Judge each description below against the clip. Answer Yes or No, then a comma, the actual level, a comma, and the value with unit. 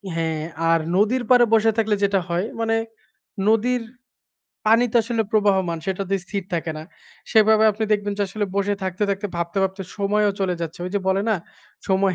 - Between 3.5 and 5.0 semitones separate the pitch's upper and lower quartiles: No, narrow, 2.5 semitones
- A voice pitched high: Yes, high, 200 Hz